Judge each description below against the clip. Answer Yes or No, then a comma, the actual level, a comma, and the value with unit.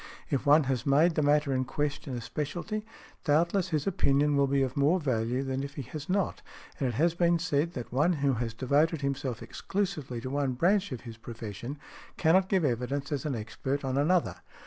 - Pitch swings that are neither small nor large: Yes, average, 3.9 semitones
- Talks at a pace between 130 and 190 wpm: No, average, 200 wpm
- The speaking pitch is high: No, medium, 140 Hz